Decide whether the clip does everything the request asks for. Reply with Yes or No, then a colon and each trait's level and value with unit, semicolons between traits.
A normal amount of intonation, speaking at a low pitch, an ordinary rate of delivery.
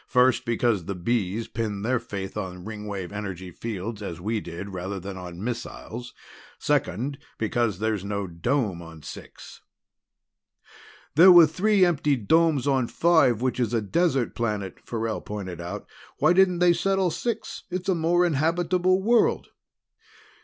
No: wide, 8.6 semitones; low, 115 Hz; average, 145 wpm